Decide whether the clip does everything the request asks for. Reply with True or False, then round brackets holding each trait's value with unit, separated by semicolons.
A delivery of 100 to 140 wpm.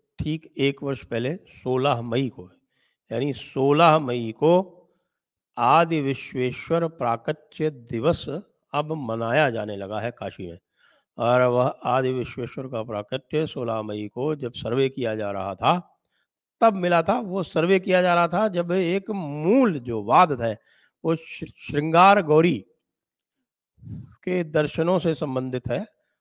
True (135 wpm)